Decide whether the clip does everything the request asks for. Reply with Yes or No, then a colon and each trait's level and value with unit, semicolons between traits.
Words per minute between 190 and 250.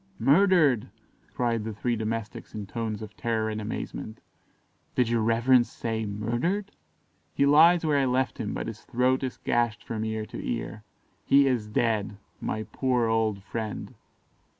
No: average, 155 wpm